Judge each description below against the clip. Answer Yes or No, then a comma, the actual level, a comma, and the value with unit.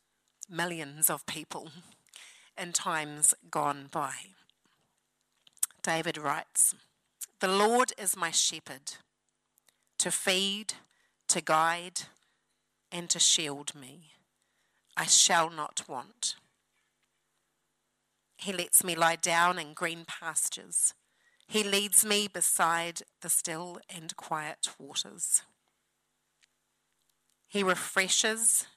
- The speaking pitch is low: No, medium, 175 Hz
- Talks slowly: Yes, slow, 95 wpm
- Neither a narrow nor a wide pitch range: Yes, average, 3.5 semitones